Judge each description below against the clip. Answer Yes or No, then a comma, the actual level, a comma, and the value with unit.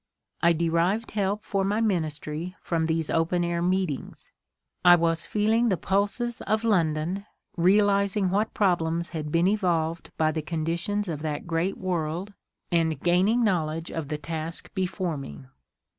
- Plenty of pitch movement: No, average, 3.5 semitones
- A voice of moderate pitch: Yes, medium, 175 Hz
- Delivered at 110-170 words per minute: Yes, average, 155 wpm